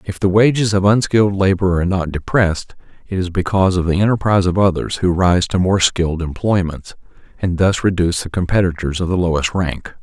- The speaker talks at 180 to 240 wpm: Yes, average, 190 wpm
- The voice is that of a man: Yes, male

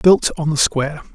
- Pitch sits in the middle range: Yes, medium, 155 Hz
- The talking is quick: Yes, fast, 210 wpm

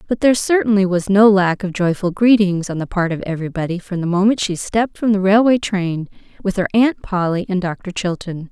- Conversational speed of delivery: No, fast, 210 wpm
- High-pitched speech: Yes, high, 195 Hz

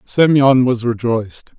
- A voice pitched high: No, low, 125 Hz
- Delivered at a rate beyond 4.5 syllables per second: No, 4.2 syllables/s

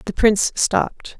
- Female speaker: Yes, female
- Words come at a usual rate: Yes, average, 150 wpm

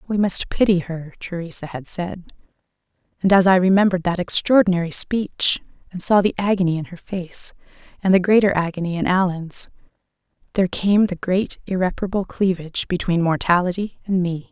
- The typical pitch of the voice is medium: Yes, medium, 180 Hz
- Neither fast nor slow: Yes, average, 155 wpm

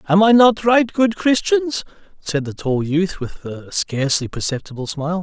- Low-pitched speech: No, medium, 180 Hz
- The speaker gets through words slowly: No, average, 170 wpm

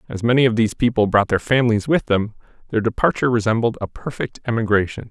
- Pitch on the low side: Yes, low, 115 Hz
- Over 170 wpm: Yes, average, 190 wpm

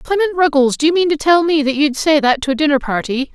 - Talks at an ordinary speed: No, fast, 285 wpm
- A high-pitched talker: Yes, very high, 295 Hz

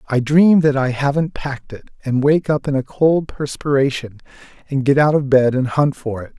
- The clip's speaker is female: No, male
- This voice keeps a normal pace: No, fast, 215 wpm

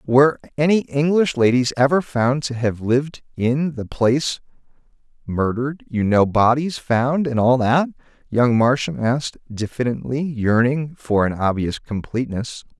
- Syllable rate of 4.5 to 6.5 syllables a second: Yes, 4.6 syllables/s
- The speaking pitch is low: Yes, low, 130 Hz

